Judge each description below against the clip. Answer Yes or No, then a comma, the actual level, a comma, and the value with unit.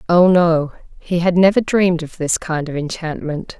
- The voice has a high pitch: No, medium, 170 Hz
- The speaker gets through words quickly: No, average, 185 wpm